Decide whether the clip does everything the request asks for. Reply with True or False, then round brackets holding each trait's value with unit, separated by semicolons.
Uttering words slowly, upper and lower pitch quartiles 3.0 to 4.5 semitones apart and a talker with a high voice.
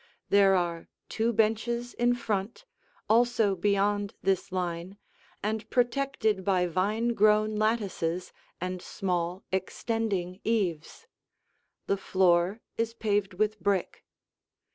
True (105 wpm; 3.3 semitones; 205 Hz)